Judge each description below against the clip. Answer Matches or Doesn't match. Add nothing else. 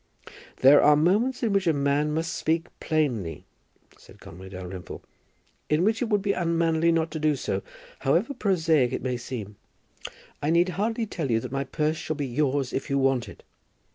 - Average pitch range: Matches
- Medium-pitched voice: Matches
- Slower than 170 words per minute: Doesn't match